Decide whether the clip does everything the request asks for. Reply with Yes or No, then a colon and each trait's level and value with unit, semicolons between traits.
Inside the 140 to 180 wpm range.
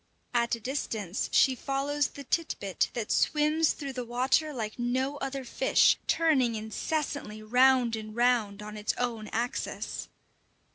Yes: average, 145 wpm